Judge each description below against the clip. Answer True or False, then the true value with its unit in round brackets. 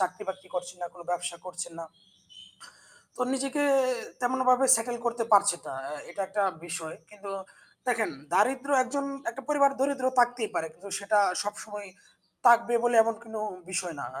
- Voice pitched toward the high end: True (215 Hz)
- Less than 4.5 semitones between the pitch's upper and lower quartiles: False (5.3 semitones)